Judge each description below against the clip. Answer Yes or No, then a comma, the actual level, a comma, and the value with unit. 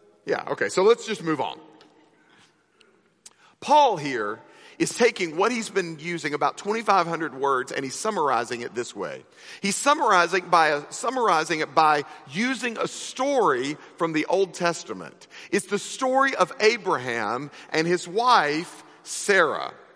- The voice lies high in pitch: Yes, high, 195 Hz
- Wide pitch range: Yes, wide, 8.4 semitones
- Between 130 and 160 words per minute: Yes, average, 140 wpm